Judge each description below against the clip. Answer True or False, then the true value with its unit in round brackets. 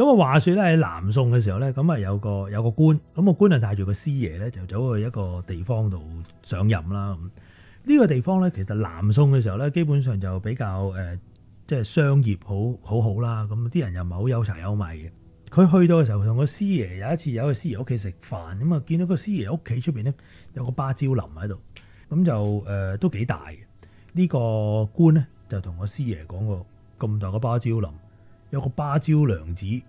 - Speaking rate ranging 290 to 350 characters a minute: True (305 characters per minute)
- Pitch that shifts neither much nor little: False (6.3 semitones)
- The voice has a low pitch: True (110 Hz)